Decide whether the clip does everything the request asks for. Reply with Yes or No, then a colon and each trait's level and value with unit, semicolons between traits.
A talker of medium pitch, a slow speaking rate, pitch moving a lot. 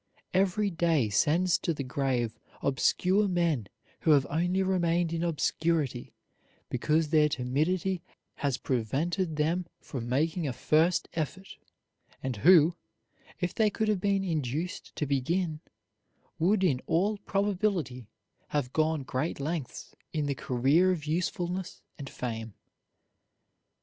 No: medium, 160 Hz; slow, 125 wpm; average, 4.8 semitones